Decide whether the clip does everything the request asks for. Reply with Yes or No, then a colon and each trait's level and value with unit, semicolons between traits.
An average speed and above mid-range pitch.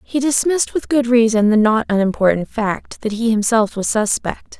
Yes: average, 185 wpm; high, 230 Hz